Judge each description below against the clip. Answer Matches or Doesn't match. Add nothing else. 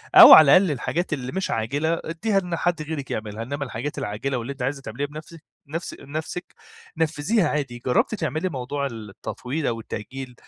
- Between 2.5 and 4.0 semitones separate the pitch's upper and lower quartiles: Doesn't match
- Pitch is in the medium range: Matches